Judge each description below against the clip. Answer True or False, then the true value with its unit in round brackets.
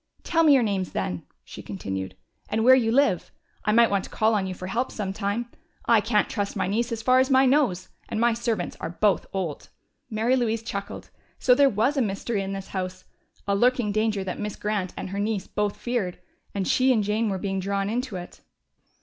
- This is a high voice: True (210 Hz)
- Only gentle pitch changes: False (3.5 semitones)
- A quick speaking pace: True (215 wpm)